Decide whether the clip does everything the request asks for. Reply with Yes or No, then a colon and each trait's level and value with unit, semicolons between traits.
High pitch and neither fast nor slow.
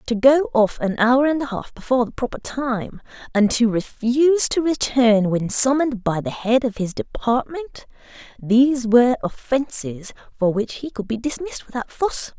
Yes: high, 245 Hz; average, 170 wpm